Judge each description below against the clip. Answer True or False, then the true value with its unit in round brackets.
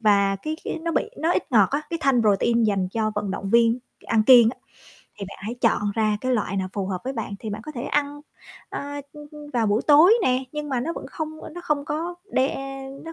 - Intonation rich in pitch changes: True (6.0 semitones)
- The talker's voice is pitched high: True (245 Hz)